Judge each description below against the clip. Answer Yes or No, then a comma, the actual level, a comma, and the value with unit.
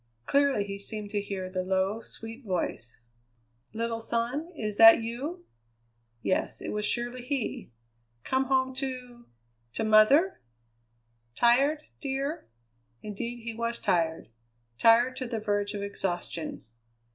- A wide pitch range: No, average, 4.1 semitones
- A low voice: No, high, 230 Hz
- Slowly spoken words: Yes, slow, 125 wpm